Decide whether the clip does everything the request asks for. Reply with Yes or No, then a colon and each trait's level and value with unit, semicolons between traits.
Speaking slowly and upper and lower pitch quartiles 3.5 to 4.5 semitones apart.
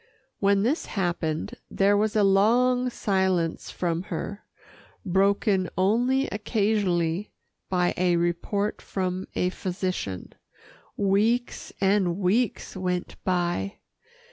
No: slow, 100 wpm; average, 2.7 semitones